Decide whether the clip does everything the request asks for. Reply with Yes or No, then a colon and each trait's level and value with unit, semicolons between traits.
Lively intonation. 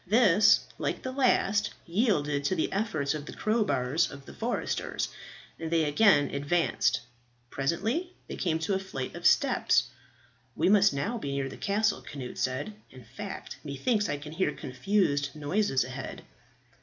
Yes: wide, 6.7 semitones